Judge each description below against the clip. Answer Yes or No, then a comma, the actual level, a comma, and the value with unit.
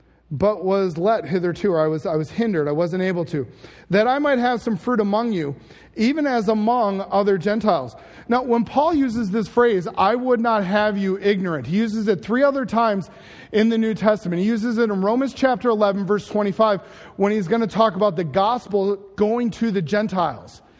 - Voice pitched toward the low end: No, high, 210 Hz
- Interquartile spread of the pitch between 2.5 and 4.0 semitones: Yes, average, 3.2 semitones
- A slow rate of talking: No, average, 200 wpm